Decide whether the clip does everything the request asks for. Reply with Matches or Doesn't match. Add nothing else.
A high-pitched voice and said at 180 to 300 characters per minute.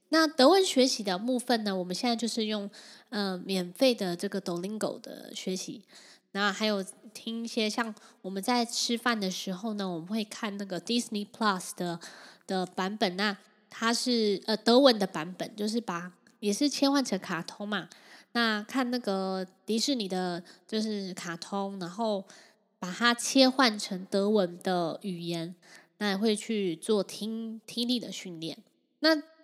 Matches